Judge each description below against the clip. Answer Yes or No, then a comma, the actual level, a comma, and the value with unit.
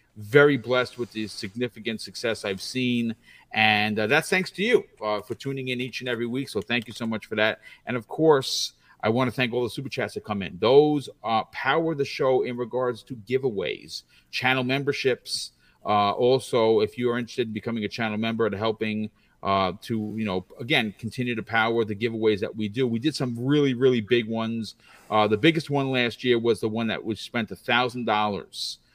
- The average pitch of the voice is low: Yes, low, 120 Hz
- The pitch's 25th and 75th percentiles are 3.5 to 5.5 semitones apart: No, average, 3.1 semitones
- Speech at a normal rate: No, fast, 210 wpm